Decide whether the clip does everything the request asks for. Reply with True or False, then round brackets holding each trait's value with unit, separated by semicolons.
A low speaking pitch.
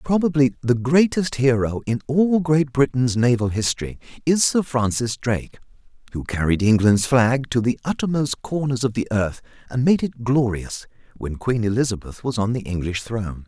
True (125 Hz)